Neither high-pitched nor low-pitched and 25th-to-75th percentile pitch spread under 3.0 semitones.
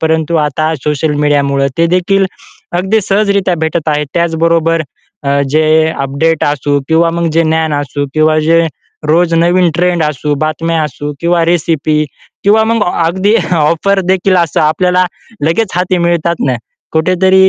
Yes: medium, 165 Hz; narrow, 2.5 semitones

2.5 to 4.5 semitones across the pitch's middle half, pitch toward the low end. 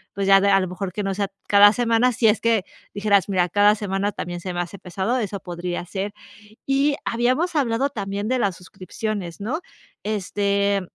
No: average, 2.9 semitones; high, 200 Hz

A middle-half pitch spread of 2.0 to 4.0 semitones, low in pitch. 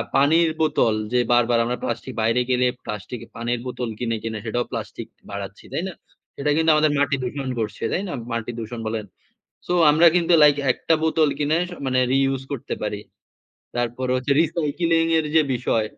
No: average, 4.7 semitones; low, 125 Hz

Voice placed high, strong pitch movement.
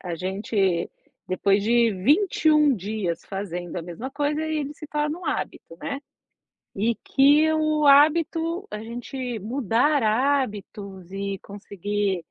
Yes: high, 230 Hz; wide, 7.1 semitones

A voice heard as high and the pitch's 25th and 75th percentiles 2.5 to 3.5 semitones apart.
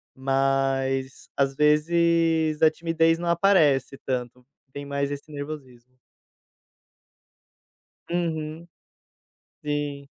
No: medium, 145 Hz; average, 3.2 semitones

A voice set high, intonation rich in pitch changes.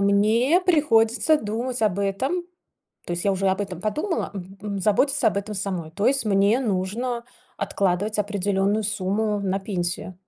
No: high, 205 Hz; average, 2.8 semitones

